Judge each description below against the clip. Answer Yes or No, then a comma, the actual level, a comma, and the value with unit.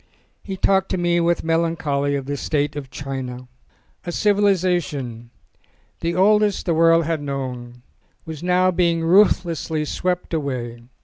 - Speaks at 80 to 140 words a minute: Yes, slow, 135 wpm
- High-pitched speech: No, medium, 165 Hz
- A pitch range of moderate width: Yes, average, 4.3 semitones